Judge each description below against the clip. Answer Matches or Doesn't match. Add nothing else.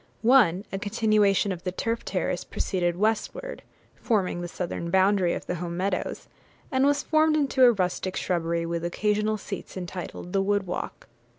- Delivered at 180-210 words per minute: Doesn't match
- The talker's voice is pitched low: Doesn't match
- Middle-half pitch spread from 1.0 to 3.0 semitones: Doesn't match